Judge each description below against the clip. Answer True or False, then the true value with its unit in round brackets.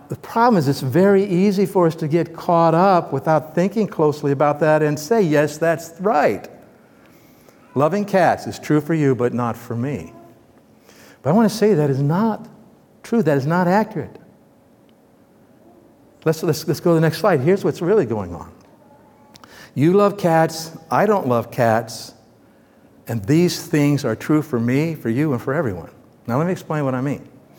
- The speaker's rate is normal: True (185 wpm)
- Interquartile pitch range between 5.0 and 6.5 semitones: False (4.6 semitones)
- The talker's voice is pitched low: False (160 Hz)